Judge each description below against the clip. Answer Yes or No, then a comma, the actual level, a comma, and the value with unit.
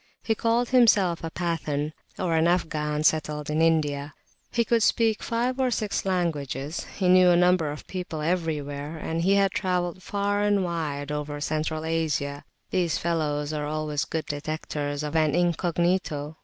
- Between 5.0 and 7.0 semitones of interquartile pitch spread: No, average, 3.5 semitones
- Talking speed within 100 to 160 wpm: Yes, average, 155 wpm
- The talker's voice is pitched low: No, medium, 160 Hz